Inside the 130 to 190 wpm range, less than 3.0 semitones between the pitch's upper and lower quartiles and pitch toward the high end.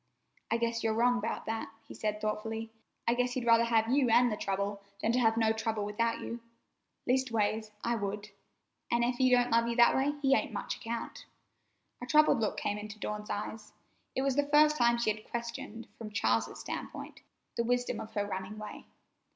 No: average, 200 wpm; narrow, 2.4 semitones; high, 230 Hz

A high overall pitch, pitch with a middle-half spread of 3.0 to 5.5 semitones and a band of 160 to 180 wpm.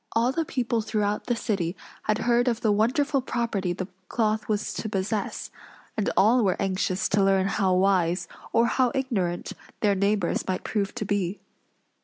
Yes: high, 210 Hz; average, 3.4 semitones; average, 170 wpm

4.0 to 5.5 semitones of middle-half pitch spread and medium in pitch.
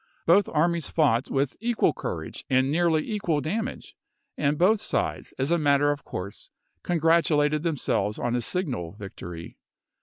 Yes: average, 4.5 semitones; medium, 150 Hz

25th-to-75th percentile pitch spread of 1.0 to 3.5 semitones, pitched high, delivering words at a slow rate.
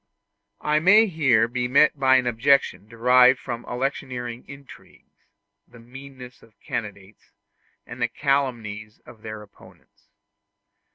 No: average, 3.1 semitones; low, 125 Hz; slow, 120 wpm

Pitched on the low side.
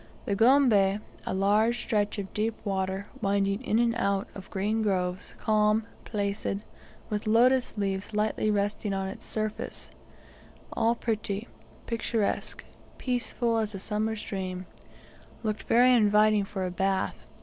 No: high, 210 Hz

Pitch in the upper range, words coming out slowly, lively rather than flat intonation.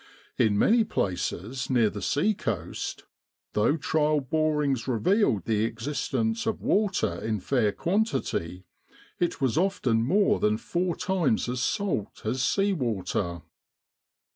No: low, 130 Hz; slow, 125 wpm; wide, 8.1 semitones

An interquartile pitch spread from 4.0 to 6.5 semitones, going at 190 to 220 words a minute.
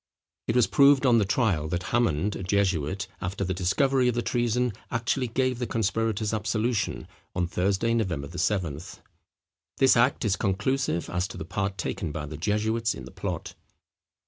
No: average, 4.8 semitones; average, 170 wpm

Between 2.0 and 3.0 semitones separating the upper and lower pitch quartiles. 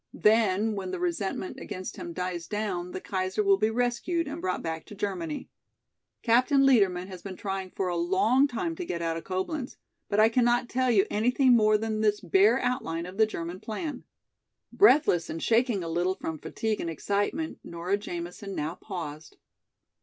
No: average, 4.7 semitones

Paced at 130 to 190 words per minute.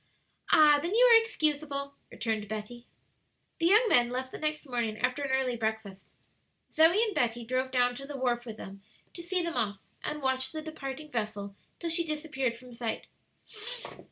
Yes: average, 180 wpm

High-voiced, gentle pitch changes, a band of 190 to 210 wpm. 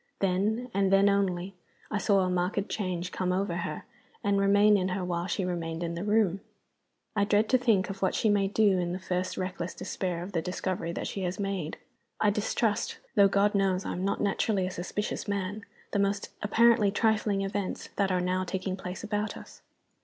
Yes: high, 195 Hz; narrow, 2.0 semitones; average, 200 wpm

